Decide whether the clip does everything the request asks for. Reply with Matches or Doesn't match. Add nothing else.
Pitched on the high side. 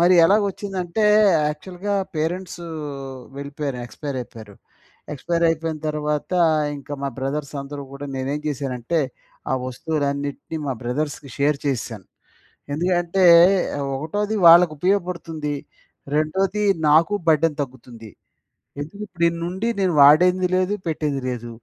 Doesn't match